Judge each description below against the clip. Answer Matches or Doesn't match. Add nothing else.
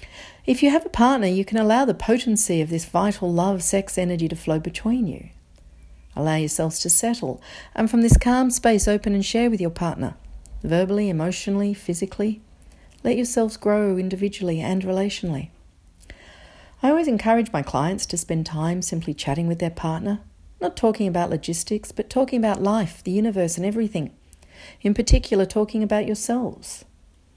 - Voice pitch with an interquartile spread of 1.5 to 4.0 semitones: Doesn't match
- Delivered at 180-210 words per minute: Doesn't match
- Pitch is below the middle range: Doesn't match